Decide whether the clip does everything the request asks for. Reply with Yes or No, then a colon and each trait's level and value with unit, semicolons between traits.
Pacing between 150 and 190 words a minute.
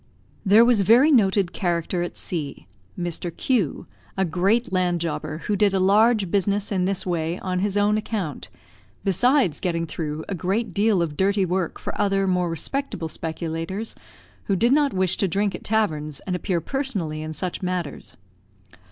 Yes: average, 170 wpm